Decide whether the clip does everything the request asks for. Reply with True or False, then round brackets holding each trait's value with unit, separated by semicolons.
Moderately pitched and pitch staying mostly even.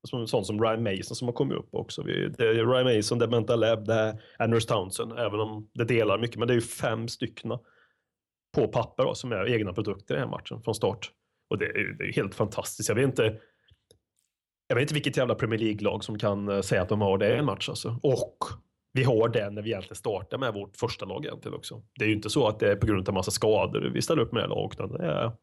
False (115 Hz; 2.0 semitones)